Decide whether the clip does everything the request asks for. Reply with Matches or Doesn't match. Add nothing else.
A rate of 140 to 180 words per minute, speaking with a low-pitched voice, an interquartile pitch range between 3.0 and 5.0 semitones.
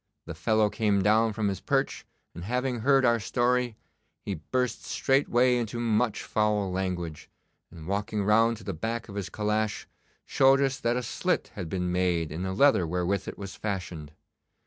Matches